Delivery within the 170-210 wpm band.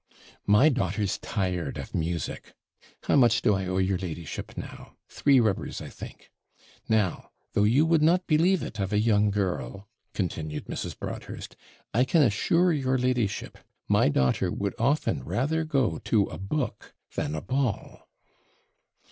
No: average, 150 wpm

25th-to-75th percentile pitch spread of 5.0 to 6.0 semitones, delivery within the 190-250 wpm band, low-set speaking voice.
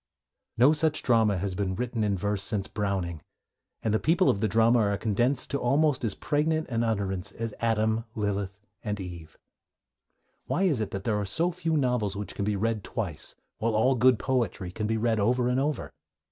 No: average, 3.6 semitones; average, 195 wpm; low, 110 Hz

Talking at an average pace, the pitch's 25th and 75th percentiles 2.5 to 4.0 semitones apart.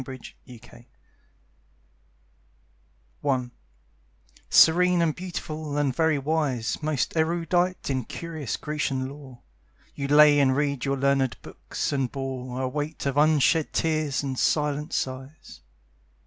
No: slow, 120 wpm; average, 2.9 semitones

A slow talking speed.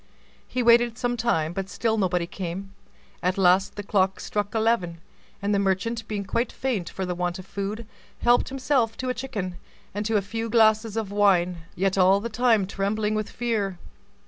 No: average, 185 wpm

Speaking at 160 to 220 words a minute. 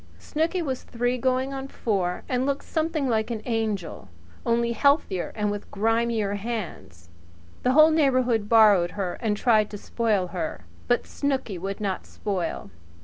No: average, 150 wpm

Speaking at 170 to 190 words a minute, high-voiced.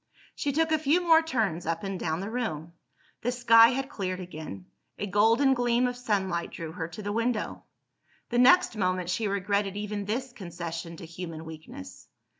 Yes: average, 180 wpm; high, 205 Hz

